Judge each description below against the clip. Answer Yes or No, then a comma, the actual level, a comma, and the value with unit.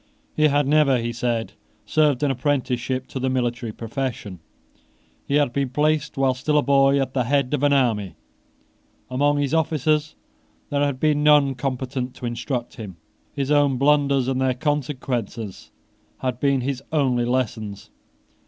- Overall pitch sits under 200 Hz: Yes, low, 135 Hz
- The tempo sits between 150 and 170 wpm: Yes, average, 155 wpm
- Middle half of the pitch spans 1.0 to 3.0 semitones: Yes, average, 2.7 semitones